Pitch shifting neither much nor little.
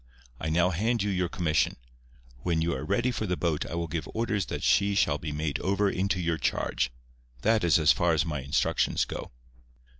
Yes: average, 4.2 semitones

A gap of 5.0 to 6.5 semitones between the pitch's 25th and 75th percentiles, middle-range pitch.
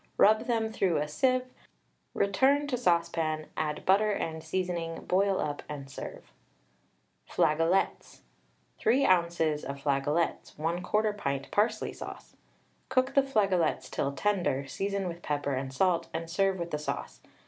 Yes: average, 5.3 semitones; medium, 175 Hz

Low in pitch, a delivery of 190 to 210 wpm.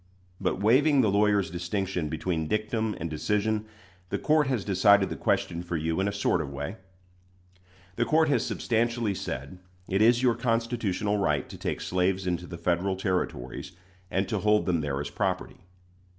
No: low, 100 Hz; average, 170 wpm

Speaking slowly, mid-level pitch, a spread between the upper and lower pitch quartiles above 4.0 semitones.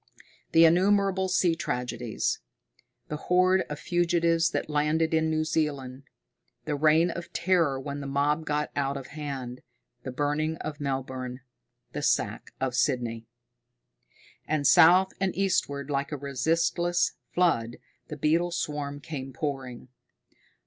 No: slow, 130 wpm; medium, 150 Hz; average, 3.5 semitones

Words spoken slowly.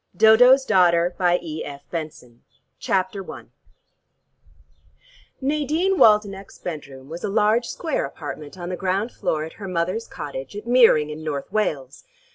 Yes: slow, 120 wpm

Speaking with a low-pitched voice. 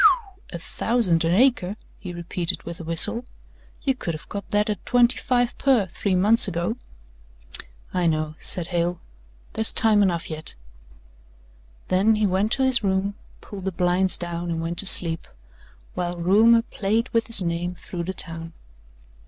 No: medium, 185 Hz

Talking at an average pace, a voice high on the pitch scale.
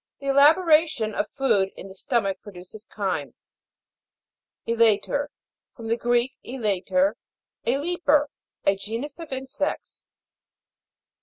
No: slow, 105 wpm; high, 240 Hz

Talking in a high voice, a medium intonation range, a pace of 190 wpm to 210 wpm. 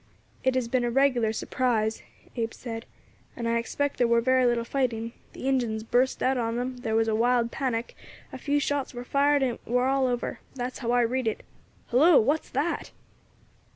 No: high, 245 Hz; narrow, 2.1 semitones; average, 195 wpm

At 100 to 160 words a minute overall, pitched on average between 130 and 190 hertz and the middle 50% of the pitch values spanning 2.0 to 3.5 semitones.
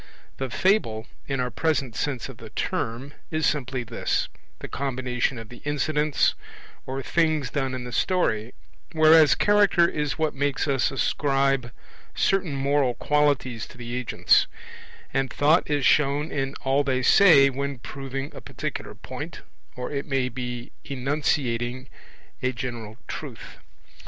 Yes: average, 140 wpm; low, 135 Hz; average, 2.9 semitones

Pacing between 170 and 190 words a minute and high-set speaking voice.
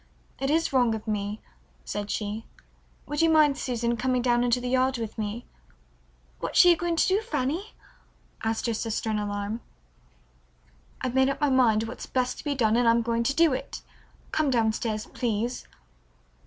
Yes: average, 180 wpm; high, 245 Hz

